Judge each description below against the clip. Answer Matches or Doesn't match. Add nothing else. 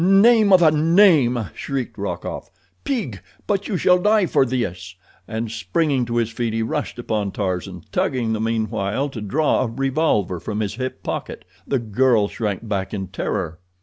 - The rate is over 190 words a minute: Doesn't match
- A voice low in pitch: Matches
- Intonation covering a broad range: Matches